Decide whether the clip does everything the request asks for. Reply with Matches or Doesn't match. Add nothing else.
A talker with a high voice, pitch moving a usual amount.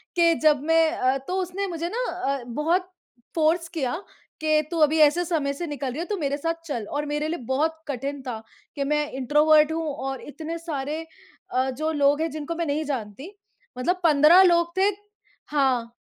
Matches